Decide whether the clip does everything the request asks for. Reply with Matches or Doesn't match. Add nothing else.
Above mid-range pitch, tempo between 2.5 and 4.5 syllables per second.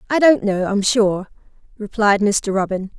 Matches